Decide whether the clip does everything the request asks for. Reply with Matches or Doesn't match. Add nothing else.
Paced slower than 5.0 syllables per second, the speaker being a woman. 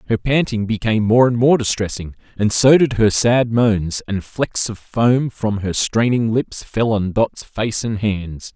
Doesn't match